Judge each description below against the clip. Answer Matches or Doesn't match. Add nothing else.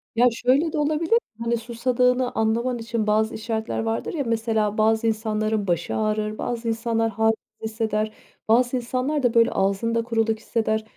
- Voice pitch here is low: Doesn't match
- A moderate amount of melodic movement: Doesn't match